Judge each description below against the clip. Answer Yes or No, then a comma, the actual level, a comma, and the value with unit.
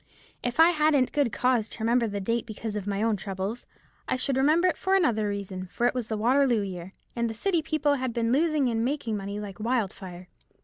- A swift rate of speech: Yes, fast, 215 wpm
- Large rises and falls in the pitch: No, average, 4.9 semitones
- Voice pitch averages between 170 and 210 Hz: No, high, 235 Hz